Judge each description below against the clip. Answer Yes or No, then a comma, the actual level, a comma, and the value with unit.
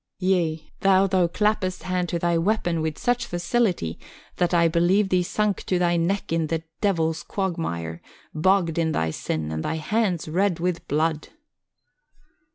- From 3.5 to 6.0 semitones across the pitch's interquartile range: No, average, 3.0 semitones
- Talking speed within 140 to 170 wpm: Yes, average, 160 wpm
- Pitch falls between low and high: Yes, medium, 175 Hz